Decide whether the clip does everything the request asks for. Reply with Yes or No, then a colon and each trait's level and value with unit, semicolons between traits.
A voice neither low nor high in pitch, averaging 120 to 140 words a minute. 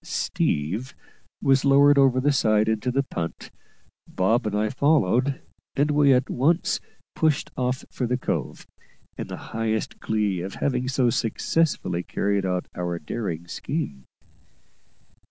No: low, 125 Hz; slow, 135 wpm